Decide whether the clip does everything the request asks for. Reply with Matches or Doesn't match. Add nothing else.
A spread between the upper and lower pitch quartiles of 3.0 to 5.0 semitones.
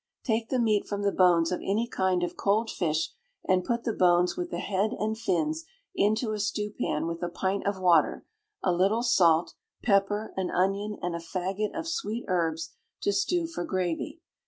Matches